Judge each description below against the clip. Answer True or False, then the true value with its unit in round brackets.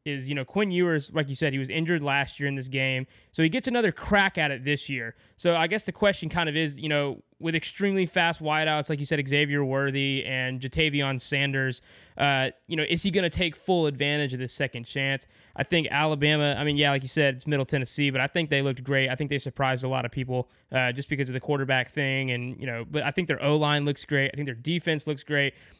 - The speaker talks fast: True (260 wpm)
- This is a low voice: False (145 Hz)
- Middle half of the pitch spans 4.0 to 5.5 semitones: False (2.7 semitones)